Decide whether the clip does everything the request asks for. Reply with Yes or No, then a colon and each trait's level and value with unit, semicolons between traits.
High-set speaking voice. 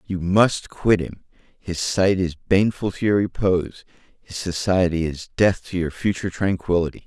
No: very low, 90 Hz